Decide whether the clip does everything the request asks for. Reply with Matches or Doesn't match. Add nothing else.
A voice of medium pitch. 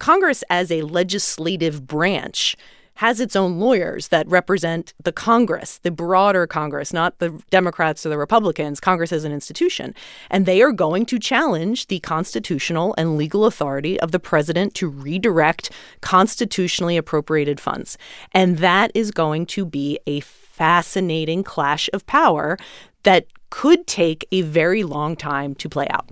Matches